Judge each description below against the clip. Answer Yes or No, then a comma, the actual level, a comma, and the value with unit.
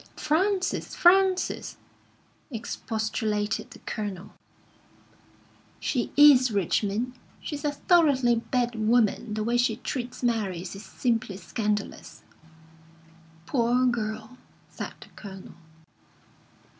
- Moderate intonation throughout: Yes, average, 3.4 semitones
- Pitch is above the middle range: Yes, high, 235 Hz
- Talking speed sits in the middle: No, slow, 95 wpm